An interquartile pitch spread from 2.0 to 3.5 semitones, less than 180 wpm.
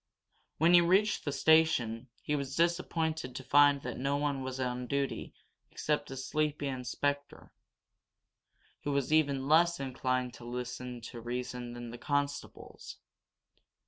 Yes: average, 3.2 semitones; average, 140 wpm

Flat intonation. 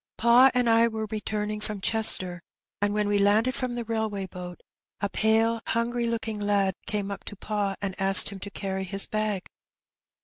Yes: narrow, 2.3 semitones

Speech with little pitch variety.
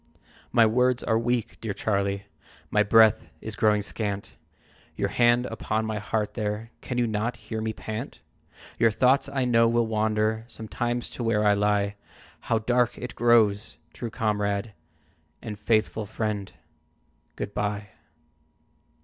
Yes: narrow, 2.1 semitones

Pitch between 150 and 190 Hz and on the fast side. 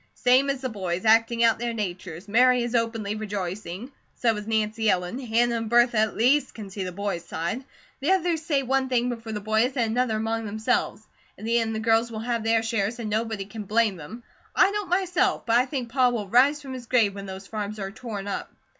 No: high, 225 Hz; fast, 225 wpm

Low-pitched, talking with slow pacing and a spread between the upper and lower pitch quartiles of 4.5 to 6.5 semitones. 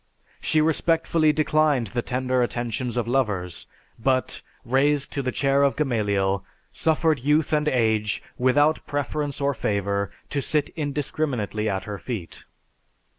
Yes: low, 130 Hz; slow, 130 wpm; average, 5.1 semitones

